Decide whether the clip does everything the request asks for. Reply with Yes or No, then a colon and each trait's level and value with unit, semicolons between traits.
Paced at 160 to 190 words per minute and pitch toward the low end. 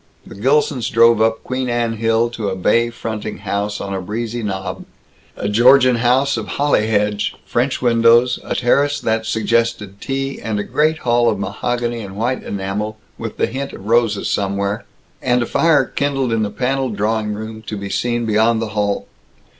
Yes: average, 180 wpm; low, 115 Hz